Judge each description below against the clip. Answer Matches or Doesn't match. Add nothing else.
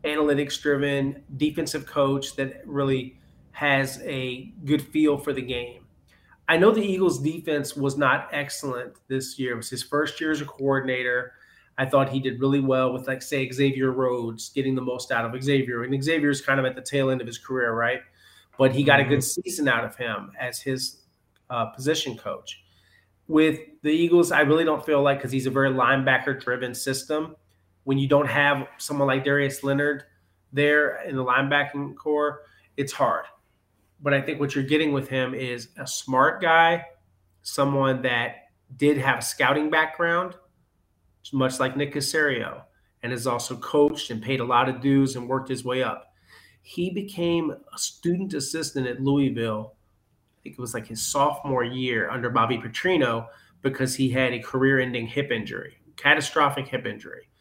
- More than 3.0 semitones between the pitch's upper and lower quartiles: Doesn't match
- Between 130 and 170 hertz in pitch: Matches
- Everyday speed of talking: Matches